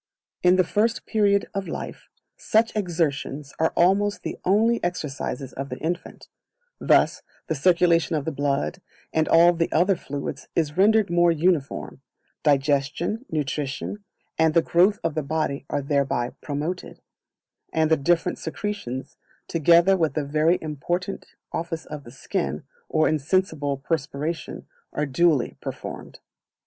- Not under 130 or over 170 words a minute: Yes, slow, 135 wpm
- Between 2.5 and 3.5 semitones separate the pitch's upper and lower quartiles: No, average, 3.9 semitones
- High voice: No, medium, 160 Hz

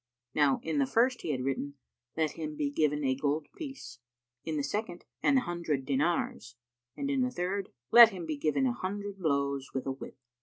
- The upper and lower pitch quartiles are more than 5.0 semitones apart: Yes, wide, 5.6 semitones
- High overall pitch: No, medium, 155 Hz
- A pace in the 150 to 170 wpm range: No, average, 195 wpm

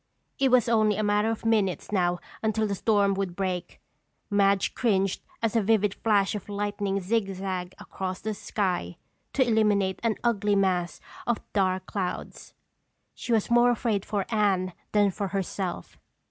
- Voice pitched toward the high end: Yes, high, 200 Hz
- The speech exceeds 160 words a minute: No, average, 155 wpm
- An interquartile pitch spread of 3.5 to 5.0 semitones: No, narrow, 2.4 semitones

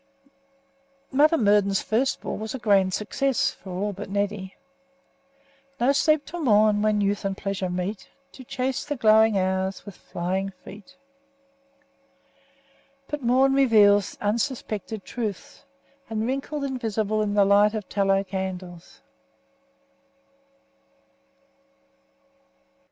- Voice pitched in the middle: No, high, 210 Hz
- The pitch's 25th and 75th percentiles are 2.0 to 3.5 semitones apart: No, average, 3.9 semitones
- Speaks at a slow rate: Yes, slow, 115 wpm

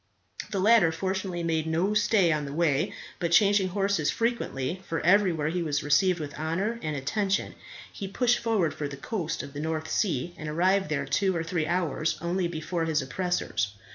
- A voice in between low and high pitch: Yes, medium, 170 Hz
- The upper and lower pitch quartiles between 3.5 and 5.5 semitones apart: Yes, average, 3.8 semitones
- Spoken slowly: No, average, 185 wpm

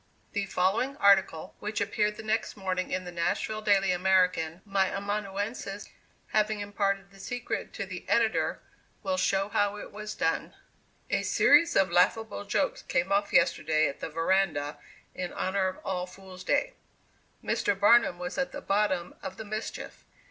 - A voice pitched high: Yes, high, 195 Hz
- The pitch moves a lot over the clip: No, narrow, 2.4 semitones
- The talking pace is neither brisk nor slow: Yes, average, 160 wpm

